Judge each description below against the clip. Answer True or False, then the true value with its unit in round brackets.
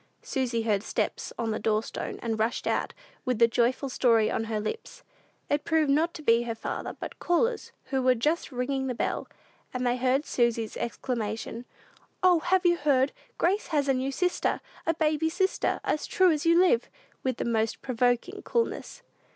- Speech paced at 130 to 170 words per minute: False (185 wpm)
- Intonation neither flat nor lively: False (5.7 semitones)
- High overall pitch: True (260 Hz)